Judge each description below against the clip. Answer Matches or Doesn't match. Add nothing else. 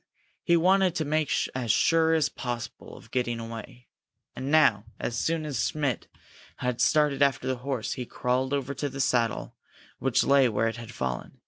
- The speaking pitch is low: Matches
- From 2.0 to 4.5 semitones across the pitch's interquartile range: Matches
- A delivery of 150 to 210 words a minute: Matches